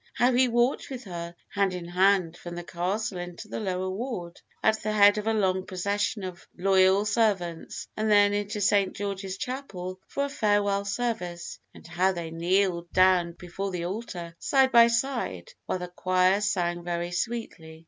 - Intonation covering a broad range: No, average, 3.3 semitones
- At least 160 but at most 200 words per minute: Yes, average, 175 wpm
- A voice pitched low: No, high, 195 Hz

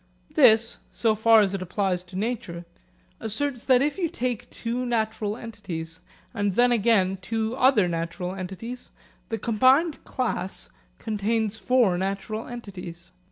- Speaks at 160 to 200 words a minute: No, slow, 135 wpm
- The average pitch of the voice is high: Yes, high, 220 Hz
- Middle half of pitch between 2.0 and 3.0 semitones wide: No, average, 4.1 semitones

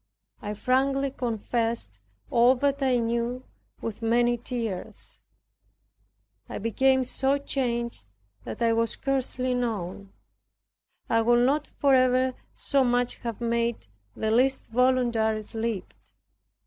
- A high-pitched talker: Yes, high, 240 Hz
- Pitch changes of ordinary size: No, narrow, 2.2 semitones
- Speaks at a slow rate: Yes, slow, 110 wpm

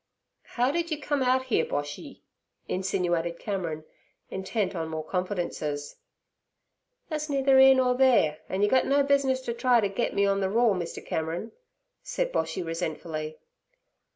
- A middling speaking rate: Yes, average, 155 wpm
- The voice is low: No, high, 200 Hz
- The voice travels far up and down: Yes, wide, 7.7 semitones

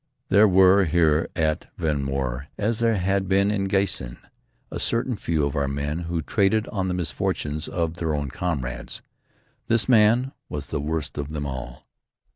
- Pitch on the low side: Yes, very low, 85 Hz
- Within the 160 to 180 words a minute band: Yes, average, 170 wpm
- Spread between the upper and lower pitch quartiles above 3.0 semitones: Yes, average, 5.3 semitones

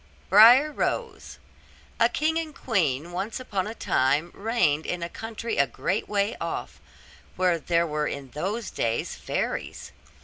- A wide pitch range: Yes, wide, 6.9 semitones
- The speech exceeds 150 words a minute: No, average, 145 wpm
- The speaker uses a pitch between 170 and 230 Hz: Yes, high, 190 Hz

